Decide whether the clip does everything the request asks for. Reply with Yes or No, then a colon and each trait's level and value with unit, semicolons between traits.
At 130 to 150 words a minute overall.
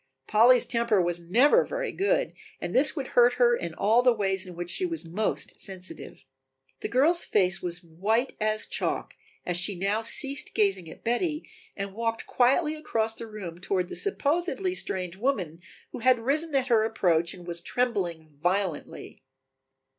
No: average, 170 wpm